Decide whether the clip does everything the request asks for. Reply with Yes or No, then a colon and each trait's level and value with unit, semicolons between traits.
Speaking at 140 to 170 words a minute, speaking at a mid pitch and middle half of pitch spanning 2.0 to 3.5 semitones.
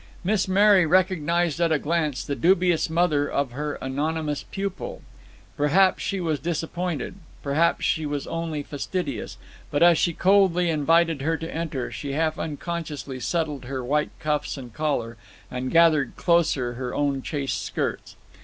Yes: average, 150 wpm; medium, 155 Hz; average, 3.1 semitones